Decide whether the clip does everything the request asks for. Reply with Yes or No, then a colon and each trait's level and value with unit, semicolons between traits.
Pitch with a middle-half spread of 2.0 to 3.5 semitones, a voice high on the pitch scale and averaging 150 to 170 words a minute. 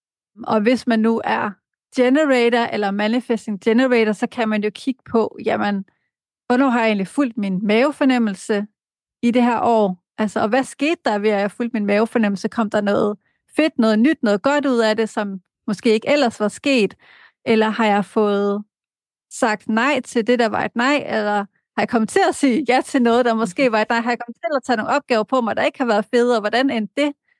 No: average, 3.2 semitones; high, 230 Hz; average, 220 wpm